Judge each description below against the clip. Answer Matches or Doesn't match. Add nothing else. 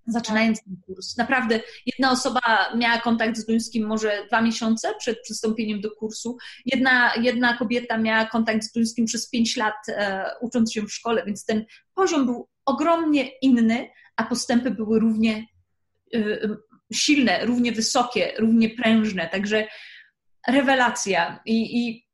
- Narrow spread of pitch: Matches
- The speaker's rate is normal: Matches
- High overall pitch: Matches